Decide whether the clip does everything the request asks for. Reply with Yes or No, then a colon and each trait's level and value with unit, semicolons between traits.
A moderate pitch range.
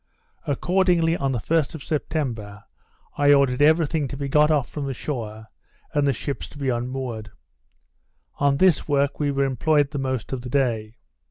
Yes: average, 3.0 semitones